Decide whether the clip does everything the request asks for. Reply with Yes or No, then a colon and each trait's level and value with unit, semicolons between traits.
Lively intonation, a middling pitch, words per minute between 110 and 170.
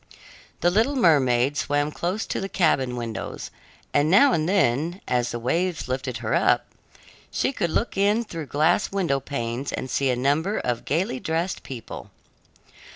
Yes: wide, 6.1 semitones; medium, 145 Hz; average, 160 wpm